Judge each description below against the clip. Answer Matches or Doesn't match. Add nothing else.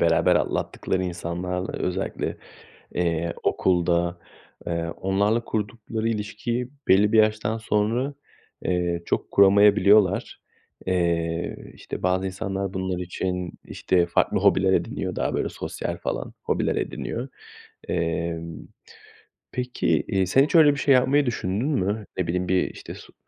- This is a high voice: Doesn't match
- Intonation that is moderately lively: Matches